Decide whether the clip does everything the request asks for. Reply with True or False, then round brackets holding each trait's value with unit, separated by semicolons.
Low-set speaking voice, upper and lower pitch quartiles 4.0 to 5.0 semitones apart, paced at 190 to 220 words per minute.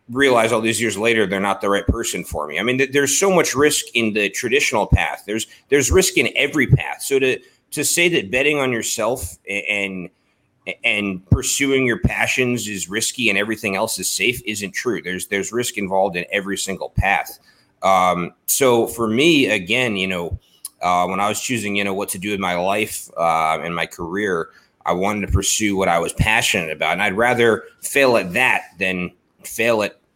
True (105 Hz; 4.4 semitones; 200 wpm)